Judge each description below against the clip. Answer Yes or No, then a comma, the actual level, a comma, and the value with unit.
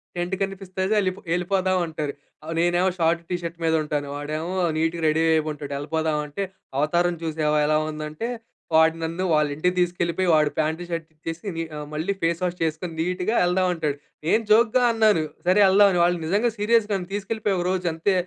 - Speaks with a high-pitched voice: No, medium, 170 Hz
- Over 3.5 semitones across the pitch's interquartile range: No, average, 3.1 semitones